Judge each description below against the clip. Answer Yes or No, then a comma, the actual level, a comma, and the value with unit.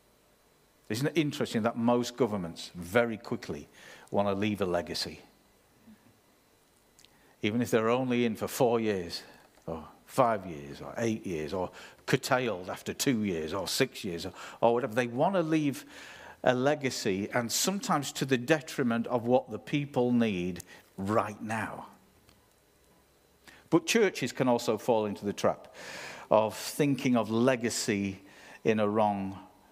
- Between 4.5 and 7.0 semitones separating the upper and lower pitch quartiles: No, average, 3.9 semitones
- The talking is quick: No, average, 145 wpm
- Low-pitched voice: Yes, low, 115 Hz